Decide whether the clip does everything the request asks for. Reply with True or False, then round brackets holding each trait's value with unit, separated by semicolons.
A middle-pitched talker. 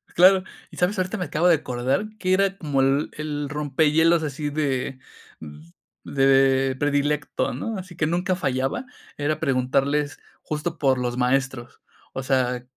True (145 Hz)